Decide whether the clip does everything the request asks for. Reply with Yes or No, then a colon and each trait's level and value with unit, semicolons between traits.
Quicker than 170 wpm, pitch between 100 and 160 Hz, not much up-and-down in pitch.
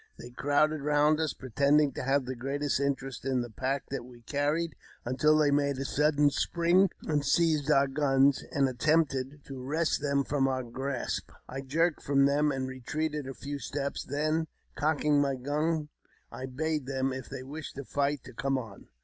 Yes: average, 185 wpm; medium, 140 Hz; narrow, 2.1 semitones